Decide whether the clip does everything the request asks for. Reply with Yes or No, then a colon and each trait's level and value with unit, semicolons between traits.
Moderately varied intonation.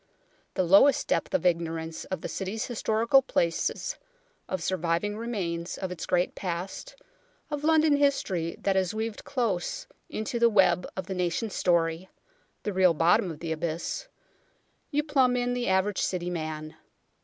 No: wide, 5.7 semitones